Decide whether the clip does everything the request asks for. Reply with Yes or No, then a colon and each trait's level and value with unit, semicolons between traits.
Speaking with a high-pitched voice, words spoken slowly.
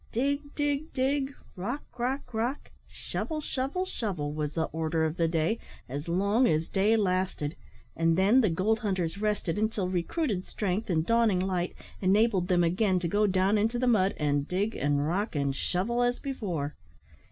No: high, 195 Hz; average, 170 wpm